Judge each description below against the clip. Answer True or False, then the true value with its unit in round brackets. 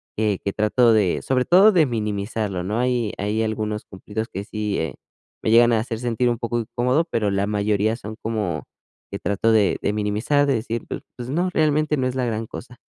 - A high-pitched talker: False (110 Hz)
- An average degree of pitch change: True (3.0 semitones)